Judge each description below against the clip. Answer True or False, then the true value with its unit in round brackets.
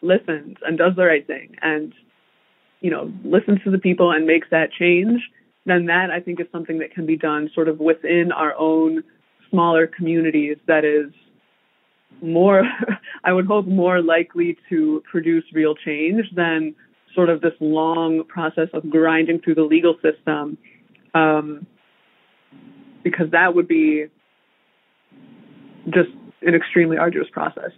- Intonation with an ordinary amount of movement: False (2.3 semitones)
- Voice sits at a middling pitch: True (165 Hz)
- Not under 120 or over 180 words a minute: True (145 wpm)